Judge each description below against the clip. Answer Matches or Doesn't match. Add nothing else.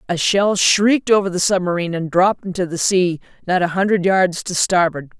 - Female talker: Matches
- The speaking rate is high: Doesn't match